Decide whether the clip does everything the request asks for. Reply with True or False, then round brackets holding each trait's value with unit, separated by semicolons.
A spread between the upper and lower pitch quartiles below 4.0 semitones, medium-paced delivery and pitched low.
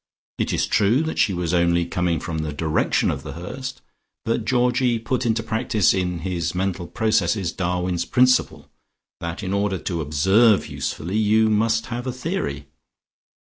False (4.9 semitones; 160 wpm; 100 Hz)